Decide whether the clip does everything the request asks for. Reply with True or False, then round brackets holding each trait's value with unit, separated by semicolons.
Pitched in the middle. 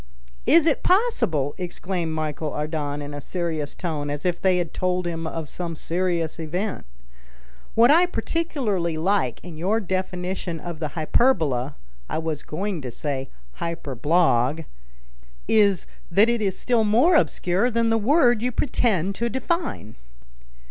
True (175 Hz)